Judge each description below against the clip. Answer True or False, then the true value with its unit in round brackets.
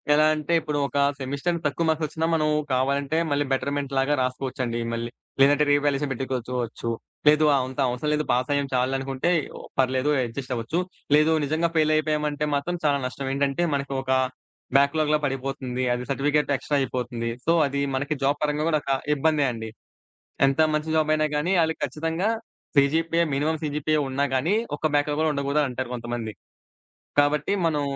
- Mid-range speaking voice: True (145 Hz)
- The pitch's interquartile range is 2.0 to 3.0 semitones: True (2.6 semitones)